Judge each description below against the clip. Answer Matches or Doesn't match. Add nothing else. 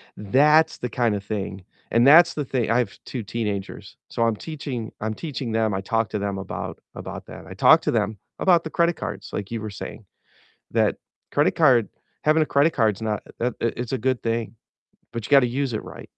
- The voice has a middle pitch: Doesn't match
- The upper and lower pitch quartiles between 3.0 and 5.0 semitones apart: Matches